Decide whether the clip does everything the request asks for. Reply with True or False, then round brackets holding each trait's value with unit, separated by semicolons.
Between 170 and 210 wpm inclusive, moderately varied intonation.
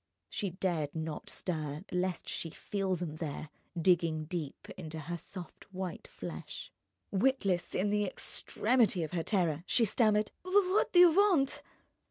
False (145 wpm; 4.6 semitones)